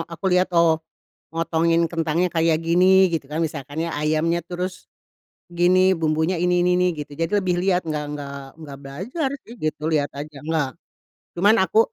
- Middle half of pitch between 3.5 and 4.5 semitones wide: No, narrow, 2.6 semitones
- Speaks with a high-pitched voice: No, medium, 165 Hz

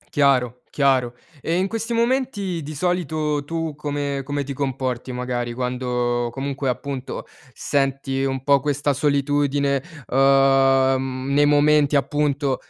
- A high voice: No, medium, 140 Hz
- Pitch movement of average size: No, narrow, 1.9 semitones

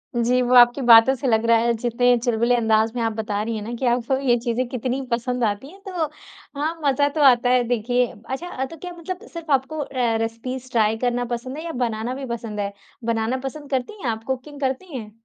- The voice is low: No, high, 245 Hz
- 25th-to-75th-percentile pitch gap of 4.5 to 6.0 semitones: No, average, 2.7 semitones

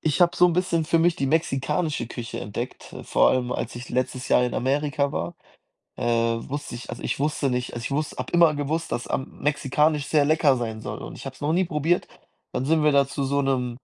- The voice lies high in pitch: No, medium, 140 Hz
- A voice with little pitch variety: No, average, 3.7 semitones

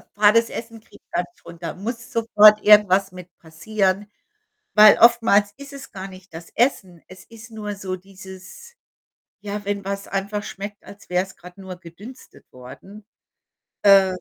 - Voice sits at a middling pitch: No, high, 200 Hz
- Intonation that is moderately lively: No, narrow, 2.3 semitones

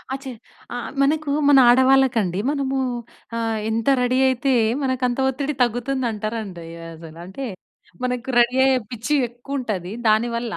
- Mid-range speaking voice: No, high, 245 Hz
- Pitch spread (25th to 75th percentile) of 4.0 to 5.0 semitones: No, average, 3.2 semitones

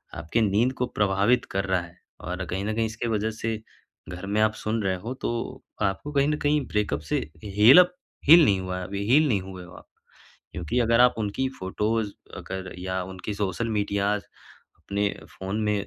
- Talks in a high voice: No, low, 105 Hz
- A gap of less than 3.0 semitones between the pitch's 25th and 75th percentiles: No, average, 3.4 semitones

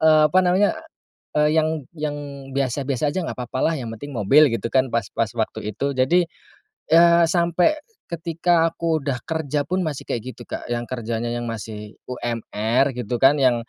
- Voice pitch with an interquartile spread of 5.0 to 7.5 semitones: Yes, average, 5.3 semitones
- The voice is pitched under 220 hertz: Yes, medium, 140 Hz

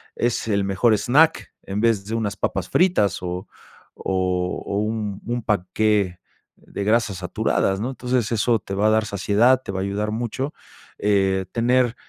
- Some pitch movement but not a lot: Yes, average, 3.3 semitones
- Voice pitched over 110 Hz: No, low, 105 Hz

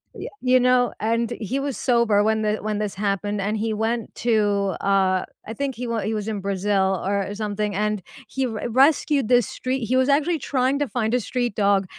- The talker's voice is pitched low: No, high, 220 Hz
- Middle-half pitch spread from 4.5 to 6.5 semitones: No, average, 3.5 semitones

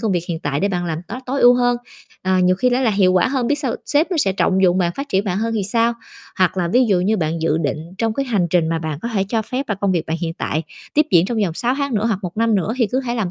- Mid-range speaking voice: No, high, 200 Hz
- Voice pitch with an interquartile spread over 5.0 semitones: Yes, wide, 5.4 semitones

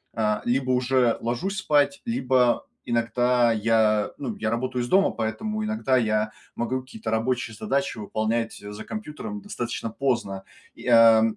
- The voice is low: Yes, low, 120 Hz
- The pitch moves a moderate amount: Yes, average, 3.2 semitones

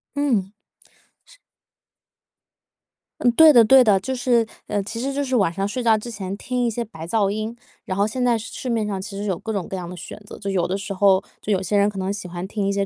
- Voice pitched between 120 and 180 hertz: No, high, 210 Hz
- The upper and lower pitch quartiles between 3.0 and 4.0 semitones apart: Yes, average, 3.5 semitones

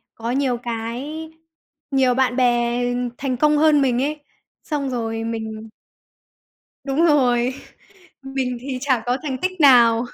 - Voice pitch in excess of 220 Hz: Yes, very high, 255 Hz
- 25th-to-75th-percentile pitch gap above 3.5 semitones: No, average, 2.8 semitones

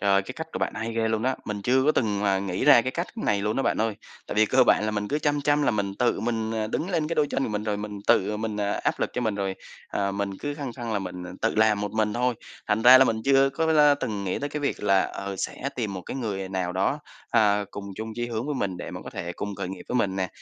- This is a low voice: Yes, low, 110 Hz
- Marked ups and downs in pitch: No, average, 4.5 semitones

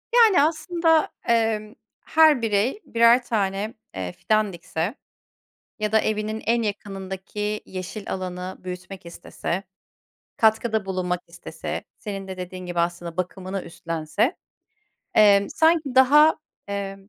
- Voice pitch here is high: Yes, high, 205 Hz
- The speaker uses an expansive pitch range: No, average, 4.0 semitones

